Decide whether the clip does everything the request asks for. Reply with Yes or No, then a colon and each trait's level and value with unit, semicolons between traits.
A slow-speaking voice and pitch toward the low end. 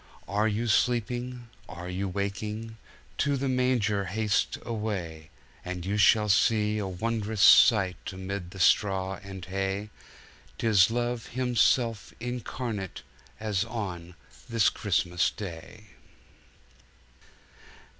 Yes: slow, 105 wpm; low, 105 Hz